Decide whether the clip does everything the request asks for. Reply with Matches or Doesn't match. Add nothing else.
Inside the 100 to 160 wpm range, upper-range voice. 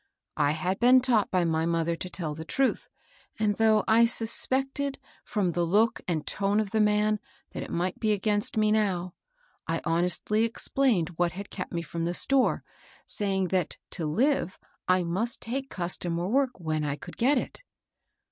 Doesn't match